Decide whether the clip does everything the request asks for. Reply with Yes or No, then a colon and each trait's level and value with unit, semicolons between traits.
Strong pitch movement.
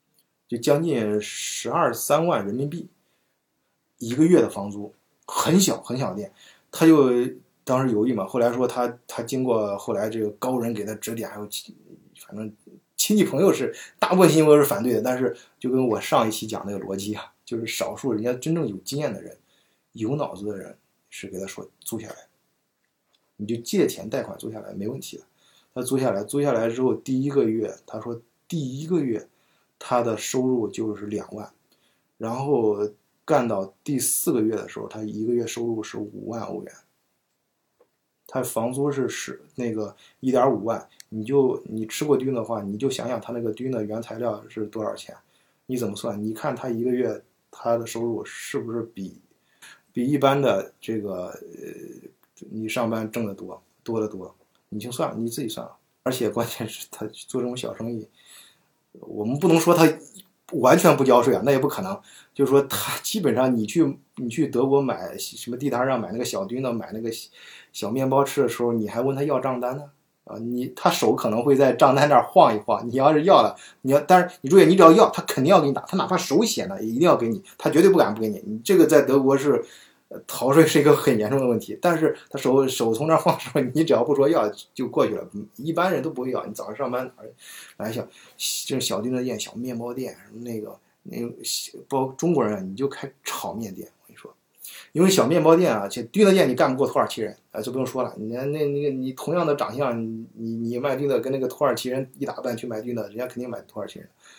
No: average, 4.3 semitones